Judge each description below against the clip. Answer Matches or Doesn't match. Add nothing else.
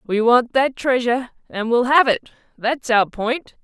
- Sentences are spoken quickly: Doesn't match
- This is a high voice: Matches